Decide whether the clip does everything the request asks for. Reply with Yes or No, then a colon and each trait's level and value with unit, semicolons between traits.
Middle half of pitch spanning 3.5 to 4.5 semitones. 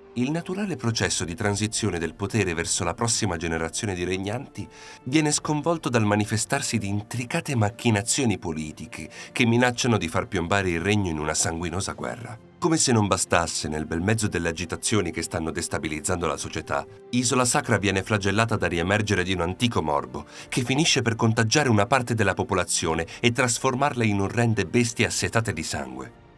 No: average, 5.3 semitones